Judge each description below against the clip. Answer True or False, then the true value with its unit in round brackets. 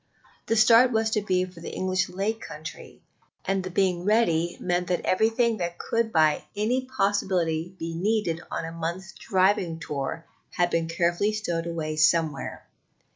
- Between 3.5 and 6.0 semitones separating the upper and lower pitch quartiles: True (4.2 semitones)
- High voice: False (180 Hz)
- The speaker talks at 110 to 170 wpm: True (160 wpm)